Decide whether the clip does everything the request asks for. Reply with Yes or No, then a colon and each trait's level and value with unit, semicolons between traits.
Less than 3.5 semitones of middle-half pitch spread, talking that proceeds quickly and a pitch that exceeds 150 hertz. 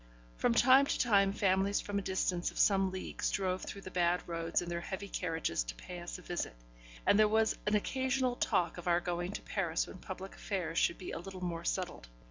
Yes: narrow, 2.6 semitones; fast, 220 wpm; medium, 185 Hz